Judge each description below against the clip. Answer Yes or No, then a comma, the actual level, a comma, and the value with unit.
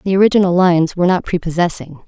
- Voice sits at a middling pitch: Yes, medium, 180 Hz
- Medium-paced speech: Yes, average, 175 wpm